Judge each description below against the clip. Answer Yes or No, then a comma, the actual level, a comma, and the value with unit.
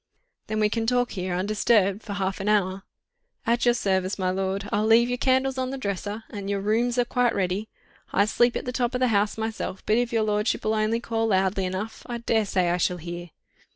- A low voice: No, high, 215 Hz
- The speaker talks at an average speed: No, fast, 220 wpm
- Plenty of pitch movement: No, average, 3.5 semitones